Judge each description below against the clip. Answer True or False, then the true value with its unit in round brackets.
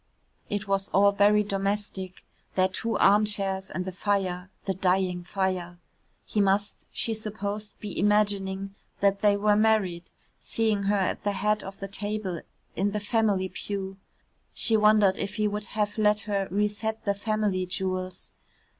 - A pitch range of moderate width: False (1.7 semitones)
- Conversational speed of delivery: True (155 wpm)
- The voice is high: True (200 Hz)